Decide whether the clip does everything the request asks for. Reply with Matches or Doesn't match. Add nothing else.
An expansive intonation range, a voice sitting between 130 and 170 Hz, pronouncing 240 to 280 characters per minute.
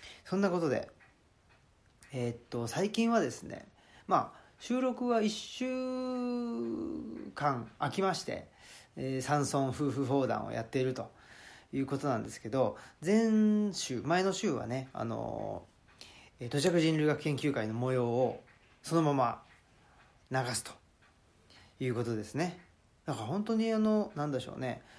Matches